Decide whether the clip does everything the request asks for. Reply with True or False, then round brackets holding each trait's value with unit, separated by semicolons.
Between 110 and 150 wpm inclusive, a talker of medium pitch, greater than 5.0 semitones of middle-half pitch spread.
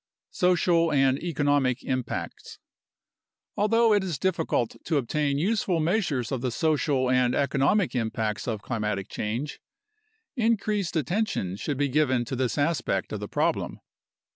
True (140 wpm; 145 Hz; 5.6 semitones)